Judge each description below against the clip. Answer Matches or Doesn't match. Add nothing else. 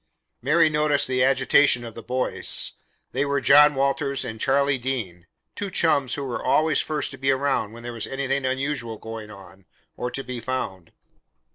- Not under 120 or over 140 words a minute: Doesn't match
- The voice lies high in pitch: Doesn't match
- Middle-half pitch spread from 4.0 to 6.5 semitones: Doesn't match